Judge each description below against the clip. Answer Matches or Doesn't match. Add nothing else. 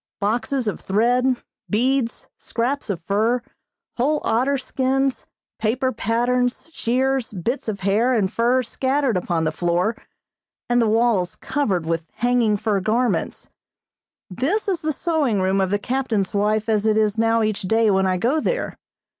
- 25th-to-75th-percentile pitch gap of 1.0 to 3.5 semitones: Doesn't match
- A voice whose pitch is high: Matches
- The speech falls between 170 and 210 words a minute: Doesn't match